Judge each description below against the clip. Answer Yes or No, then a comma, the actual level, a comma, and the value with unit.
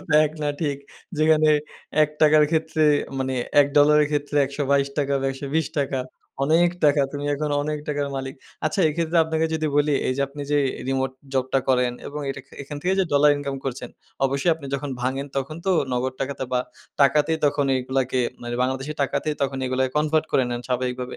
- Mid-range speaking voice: Yes, medium, 145 Hz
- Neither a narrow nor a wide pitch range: No, narrow, 2.3 semitones